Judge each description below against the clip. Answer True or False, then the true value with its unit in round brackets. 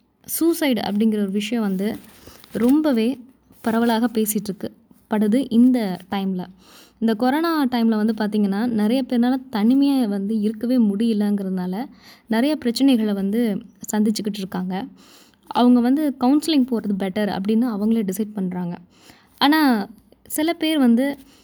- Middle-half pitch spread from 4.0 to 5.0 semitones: False (3.3 semitones)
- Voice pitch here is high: True (225 Hz)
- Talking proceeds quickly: False (110 wpm)